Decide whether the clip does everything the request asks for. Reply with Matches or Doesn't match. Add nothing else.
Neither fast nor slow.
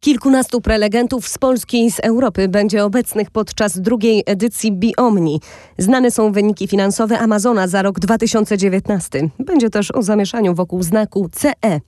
Matches